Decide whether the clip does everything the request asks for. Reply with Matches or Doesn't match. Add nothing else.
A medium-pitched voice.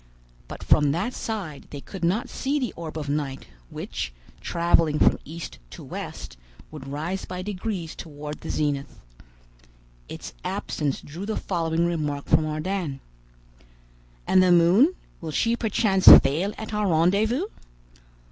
Matches